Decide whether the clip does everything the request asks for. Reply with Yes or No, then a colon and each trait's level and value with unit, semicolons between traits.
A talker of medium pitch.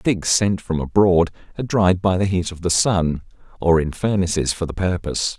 No: very low, 90 Hz